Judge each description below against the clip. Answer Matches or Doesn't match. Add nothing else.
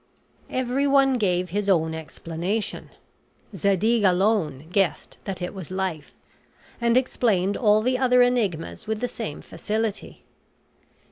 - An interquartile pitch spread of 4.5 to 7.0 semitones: Matches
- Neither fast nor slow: Doesn't match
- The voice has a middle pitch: Doesn't match